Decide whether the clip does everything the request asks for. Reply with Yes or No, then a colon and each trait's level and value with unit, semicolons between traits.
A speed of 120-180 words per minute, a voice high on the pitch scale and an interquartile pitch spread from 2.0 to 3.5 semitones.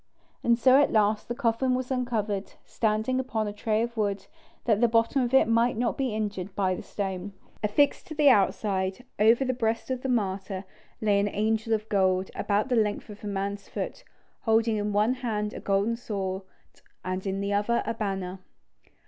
No: average, 190 wpm; high, 215 Hz; average, 2.9 semitones